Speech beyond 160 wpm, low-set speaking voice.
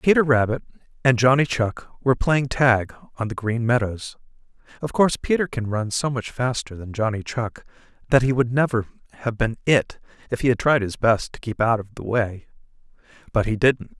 Yes: average, 195 wpm; low, 120 Hz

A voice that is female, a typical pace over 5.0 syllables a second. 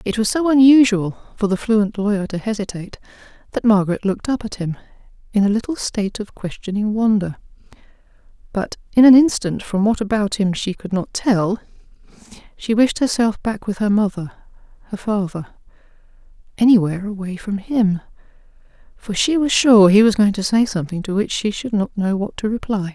Yes: female; 5.5 syllables/s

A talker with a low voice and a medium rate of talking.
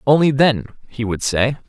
Yes: low, 130 Hz; average, 180 wpm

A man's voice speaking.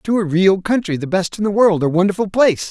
Yes: male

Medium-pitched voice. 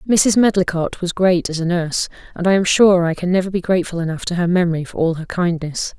Yes: medium, 175 Hz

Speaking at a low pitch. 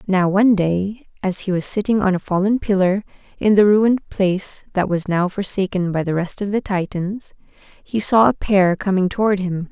No: high, 195 Hz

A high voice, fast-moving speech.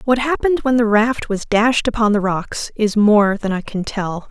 Yes: high, 220 Hz; fast, 225 wpm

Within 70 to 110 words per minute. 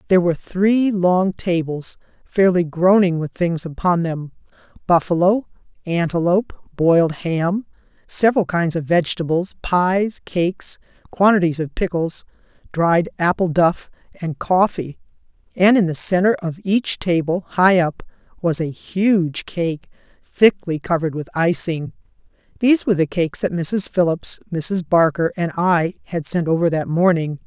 No: slow, 135 wpm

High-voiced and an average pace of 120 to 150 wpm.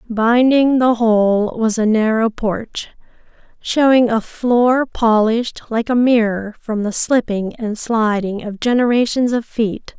Yes: high, 230 Hz; average, 140 wpm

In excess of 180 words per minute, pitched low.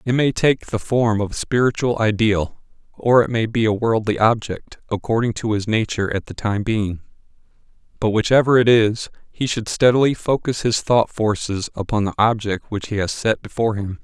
Yes: average, 190 wpm; low, 110 Hz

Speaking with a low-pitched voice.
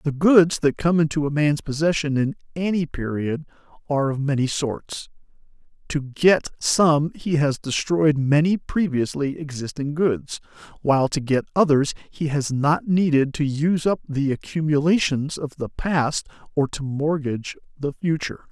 No: medium, 150 Hz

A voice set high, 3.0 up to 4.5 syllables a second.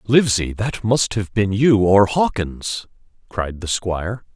No: low, 105 Hz; 4.0 syllables/s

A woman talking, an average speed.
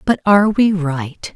Yes: female; average, 175 wpm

